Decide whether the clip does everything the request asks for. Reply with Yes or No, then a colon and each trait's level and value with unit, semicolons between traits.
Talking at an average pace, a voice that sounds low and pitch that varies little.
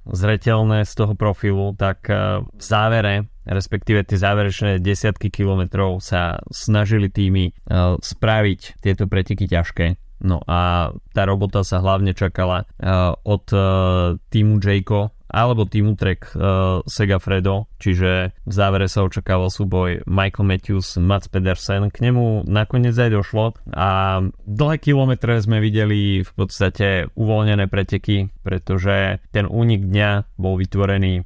Yes: average, 125 wpm; low, 100 Hz; narrow, 2.1 semitones